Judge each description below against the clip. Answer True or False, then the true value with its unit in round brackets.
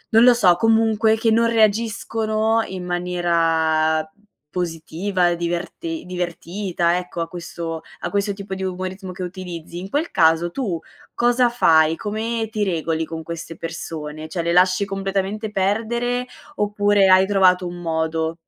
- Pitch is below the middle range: False (185 Hz)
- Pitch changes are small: False (4.2 semitones)